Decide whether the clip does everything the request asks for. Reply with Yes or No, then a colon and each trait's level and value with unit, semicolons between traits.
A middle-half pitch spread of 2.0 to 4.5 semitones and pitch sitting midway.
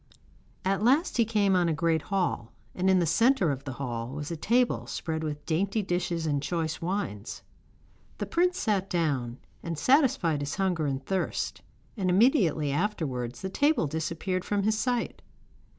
No: wide, 5.5 semitones; medium, 175 Hz